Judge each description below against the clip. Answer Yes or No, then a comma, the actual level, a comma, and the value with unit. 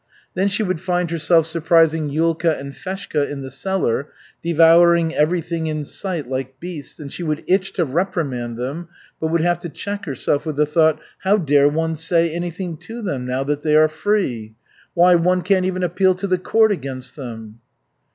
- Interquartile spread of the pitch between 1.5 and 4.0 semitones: Yes, average, 3.7 semitones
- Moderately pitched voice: Yes, medium, 165 Hz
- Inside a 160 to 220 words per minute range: Yes, average, 185 wpm